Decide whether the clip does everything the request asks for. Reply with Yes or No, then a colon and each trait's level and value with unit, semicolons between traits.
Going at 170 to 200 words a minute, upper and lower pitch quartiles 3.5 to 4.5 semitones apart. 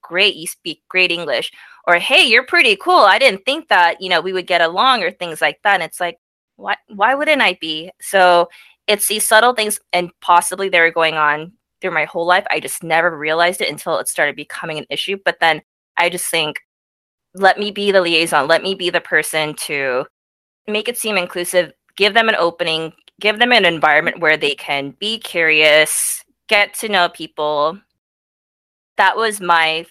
Yes: average, 195 wpm; average, 4.2 semitones